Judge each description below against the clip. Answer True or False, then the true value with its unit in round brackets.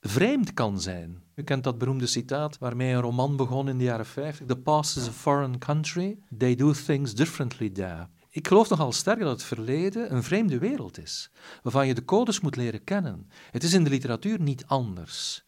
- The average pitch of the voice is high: False (135 Hz)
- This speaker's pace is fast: True (205 wpm)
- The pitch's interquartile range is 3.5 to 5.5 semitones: True (4.1 semitones)